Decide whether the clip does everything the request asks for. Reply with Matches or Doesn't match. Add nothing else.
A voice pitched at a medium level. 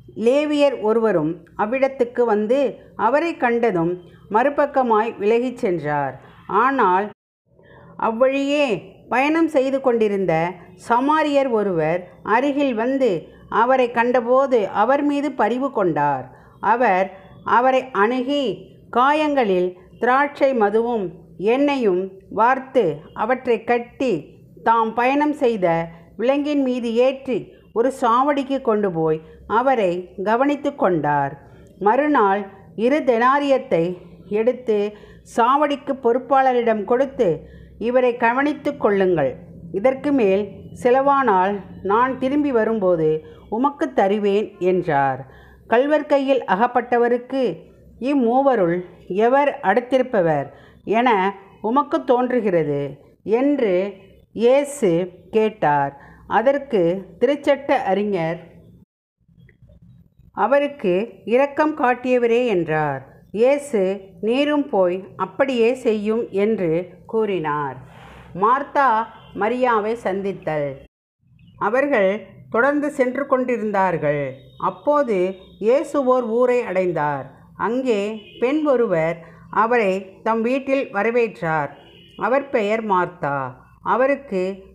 Doesn't match